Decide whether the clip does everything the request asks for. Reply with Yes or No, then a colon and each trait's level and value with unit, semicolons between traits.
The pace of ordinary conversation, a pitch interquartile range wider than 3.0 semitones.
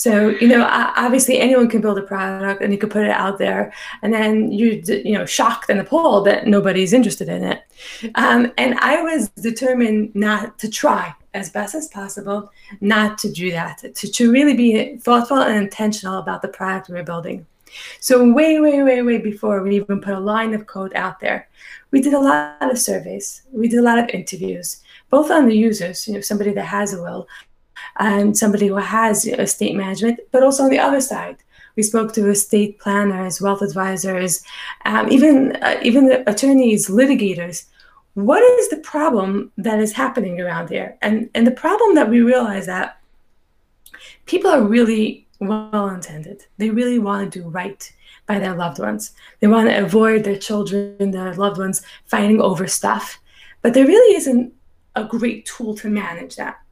Yes: average, 190 wpm; average, 3.5 semitones